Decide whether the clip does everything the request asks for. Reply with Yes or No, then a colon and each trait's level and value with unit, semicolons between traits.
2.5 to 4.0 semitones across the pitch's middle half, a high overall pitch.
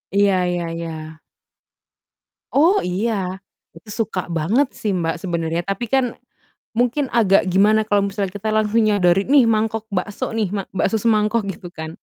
Yes: average, 3.3 semitones; high, 205 Hz